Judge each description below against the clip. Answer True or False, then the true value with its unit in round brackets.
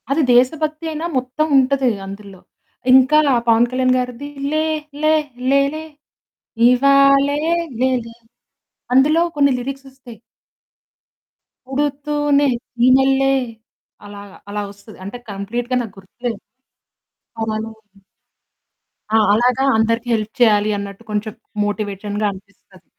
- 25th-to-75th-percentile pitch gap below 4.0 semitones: False (4.4 semitones)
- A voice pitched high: True (250 Hz)